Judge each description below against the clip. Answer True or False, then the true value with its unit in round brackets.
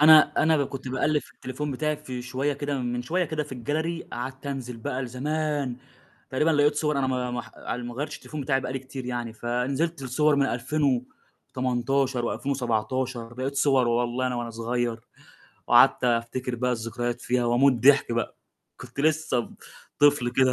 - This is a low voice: True (130 Hz)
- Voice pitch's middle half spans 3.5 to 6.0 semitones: False (3.0 semitones)